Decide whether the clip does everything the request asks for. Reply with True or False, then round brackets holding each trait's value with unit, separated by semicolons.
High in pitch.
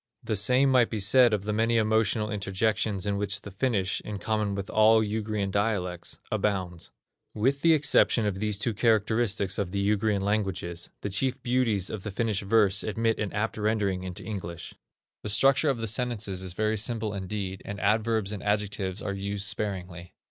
False (105 Hz)